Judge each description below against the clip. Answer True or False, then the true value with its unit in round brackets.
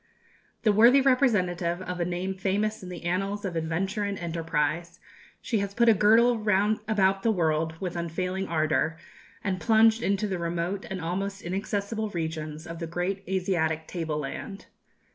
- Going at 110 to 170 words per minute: True (160 wpm)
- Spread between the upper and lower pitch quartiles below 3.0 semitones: False (3.4 semitones)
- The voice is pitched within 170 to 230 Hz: True (185 Hz)